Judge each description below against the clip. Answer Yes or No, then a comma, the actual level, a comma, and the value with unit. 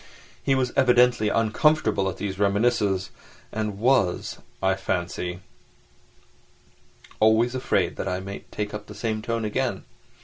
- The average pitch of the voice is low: Yes, low, 105 Hz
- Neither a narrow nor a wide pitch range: Yes, average, 3.6 semitones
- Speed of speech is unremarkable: No, slow, 130 wpm